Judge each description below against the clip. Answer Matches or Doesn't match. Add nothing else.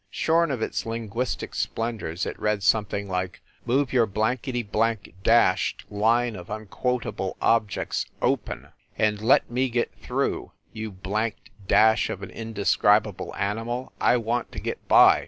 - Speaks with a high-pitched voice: Doesn't match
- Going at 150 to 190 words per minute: Doesn't match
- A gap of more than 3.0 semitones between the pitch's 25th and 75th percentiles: Doesn't match